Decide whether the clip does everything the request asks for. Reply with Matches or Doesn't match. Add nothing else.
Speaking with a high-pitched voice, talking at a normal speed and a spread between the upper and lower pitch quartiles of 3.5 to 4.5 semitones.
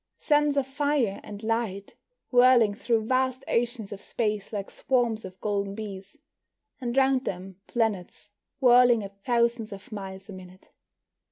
Matches